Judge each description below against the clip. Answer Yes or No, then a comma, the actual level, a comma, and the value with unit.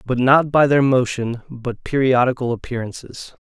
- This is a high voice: No, low, 125 Hz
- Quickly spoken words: No, average, 140 wpm